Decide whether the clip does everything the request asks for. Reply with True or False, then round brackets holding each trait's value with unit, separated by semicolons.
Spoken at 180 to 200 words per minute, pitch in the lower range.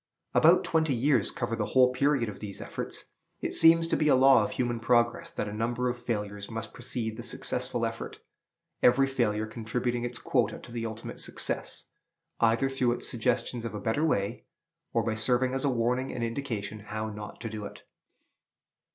True (185 wpm; 120 Hz)